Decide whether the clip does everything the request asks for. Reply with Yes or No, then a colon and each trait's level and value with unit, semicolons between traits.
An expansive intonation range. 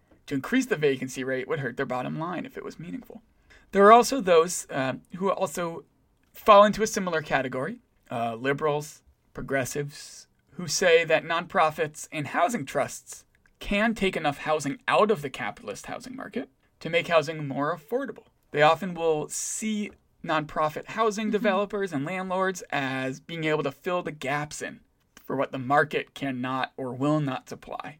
Yes: wide, 6.0 semitones